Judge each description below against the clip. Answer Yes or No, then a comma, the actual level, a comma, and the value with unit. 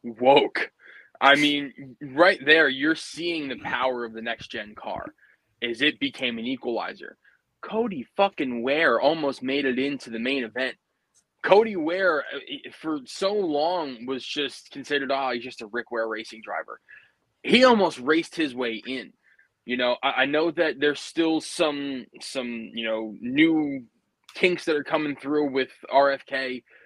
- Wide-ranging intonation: Yes, wide, 7.6 semitones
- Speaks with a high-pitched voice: No, medium, 140 Hz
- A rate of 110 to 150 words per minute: No, average, 160 wpm